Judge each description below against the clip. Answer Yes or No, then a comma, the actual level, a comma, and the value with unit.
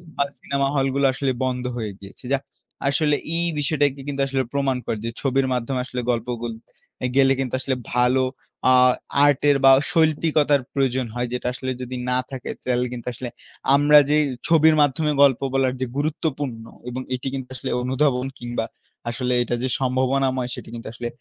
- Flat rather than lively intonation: Yes, narrow, 2.1 semitones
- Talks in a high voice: No, low, 130 Hz